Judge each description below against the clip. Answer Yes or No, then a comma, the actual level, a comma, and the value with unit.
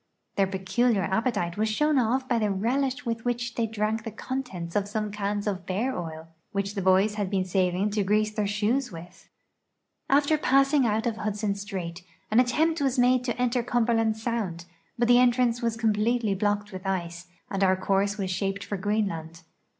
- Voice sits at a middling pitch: No, high, 210 Hz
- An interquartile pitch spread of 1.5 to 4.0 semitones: Yes, average, 3.7 semitones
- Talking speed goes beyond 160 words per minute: Yes, average, 180 wpm